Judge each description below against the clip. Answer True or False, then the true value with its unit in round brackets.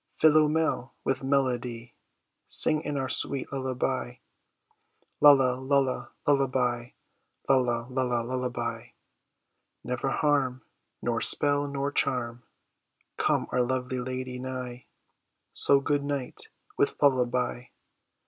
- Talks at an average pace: False (100 wpm)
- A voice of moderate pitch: False (130 Hz)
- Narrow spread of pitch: True (2.0 semitones)